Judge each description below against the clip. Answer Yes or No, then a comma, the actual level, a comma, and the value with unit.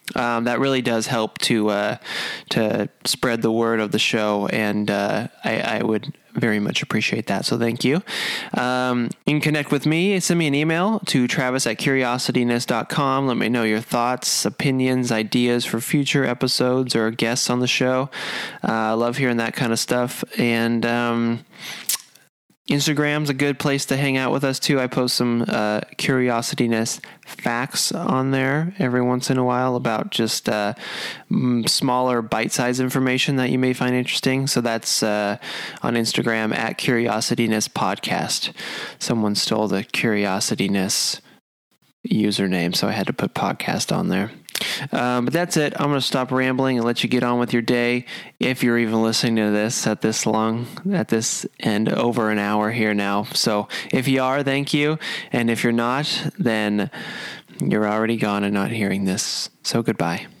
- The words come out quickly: No, average, 175 wpm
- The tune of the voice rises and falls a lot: No, average, 2.9 semitones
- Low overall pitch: Yes, low, 120 Hz